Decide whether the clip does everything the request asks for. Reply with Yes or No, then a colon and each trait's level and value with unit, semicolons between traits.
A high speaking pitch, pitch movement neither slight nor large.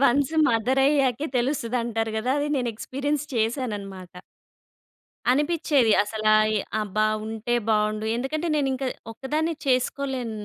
Yes: high, 245 Hz; average, 4.2 semitones